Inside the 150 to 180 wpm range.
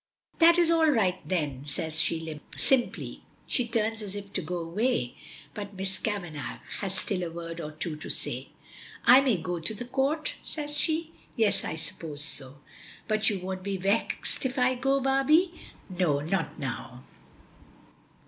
Yes: average, 165 wpm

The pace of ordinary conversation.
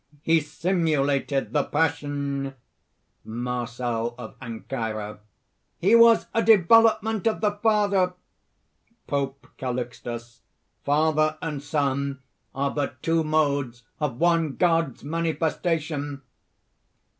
No: slow, 95 wpm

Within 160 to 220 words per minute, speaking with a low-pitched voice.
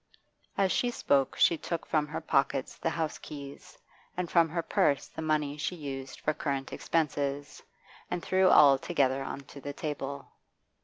No: average, 165 wpm; medium, 150 Hz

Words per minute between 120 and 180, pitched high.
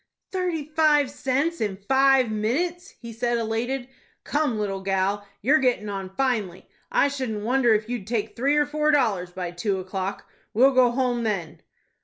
Yes: average, 165 wpm; high, 240 Hz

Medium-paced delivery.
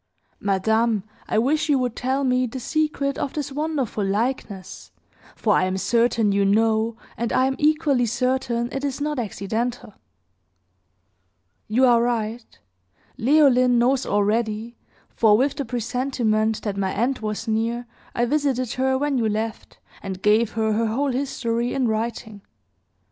Yes: average, 150 wpm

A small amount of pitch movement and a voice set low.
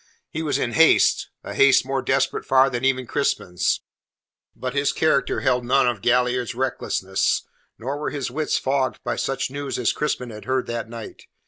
Yes: narrow, 2.1 semitones; low, 130 Hz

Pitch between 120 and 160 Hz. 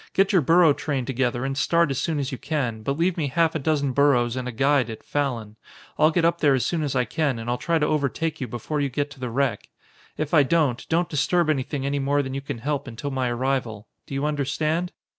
Yes: medium, 140 Hz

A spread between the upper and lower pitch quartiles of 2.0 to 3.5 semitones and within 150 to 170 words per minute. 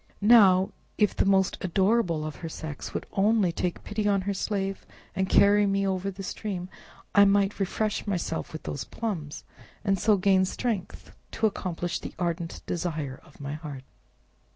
Yes: average, 2.9 semitones; average, 165 wpm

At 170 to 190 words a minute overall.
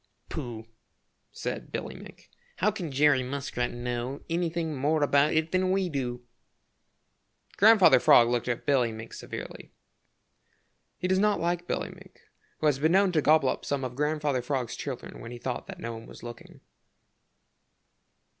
No: average, 160 wpm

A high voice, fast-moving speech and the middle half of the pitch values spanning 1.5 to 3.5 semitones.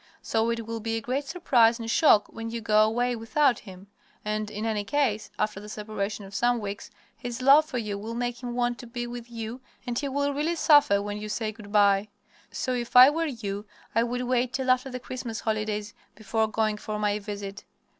Yes: high, 230 Hz; fast, 215 wpm; average, 2.8 semitones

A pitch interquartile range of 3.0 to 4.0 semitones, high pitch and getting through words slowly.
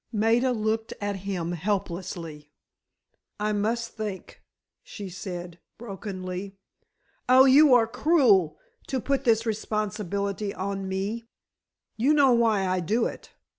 Yes: average, 3.4 semitones; high, 210 Hz; slow, 120 wpm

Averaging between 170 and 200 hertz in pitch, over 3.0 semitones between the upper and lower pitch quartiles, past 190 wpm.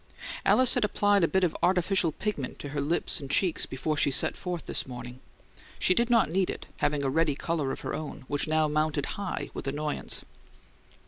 No: medium, 155 Hz; average, 4.4 semitones; average, 200 wpm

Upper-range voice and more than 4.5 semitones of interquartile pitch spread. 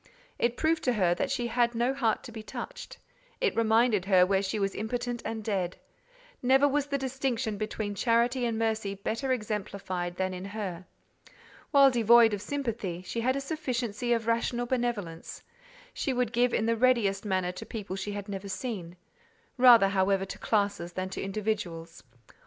No: high, 220 Hz; average, 3.9 semitones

